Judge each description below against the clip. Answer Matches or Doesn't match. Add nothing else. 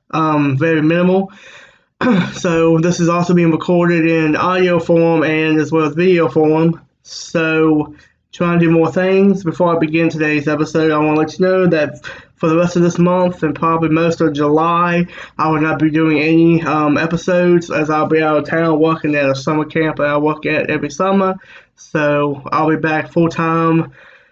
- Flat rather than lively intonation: Matches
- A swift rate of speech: Doesn't match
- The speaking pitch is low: Doesn't match